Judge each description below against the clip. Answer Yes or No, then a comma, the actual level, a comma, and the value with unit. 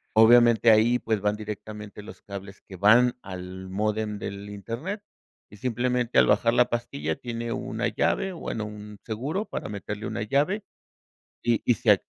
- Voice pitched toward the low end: Yes, low, 110 Hz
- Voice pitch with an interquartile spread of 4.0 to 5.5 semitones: No, average, 2.7 semitones